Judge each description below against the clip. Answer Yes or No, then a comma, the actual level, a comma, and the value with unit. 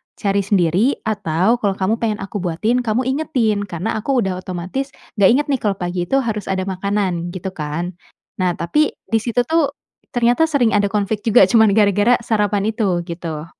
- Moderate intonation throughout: Yes, average, 4.0 semitones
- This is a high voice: Yes, high, 205 Hz